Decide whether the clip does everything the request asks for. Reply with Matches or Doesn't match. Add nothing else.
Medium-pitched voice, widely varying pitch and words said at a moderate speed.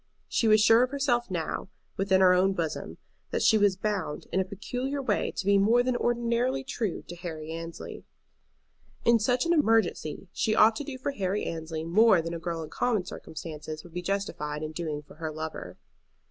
Doesn't match